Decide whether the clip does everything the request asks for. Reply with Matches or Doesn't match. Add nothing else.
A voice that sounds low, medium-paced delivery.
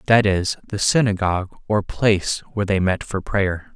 Matches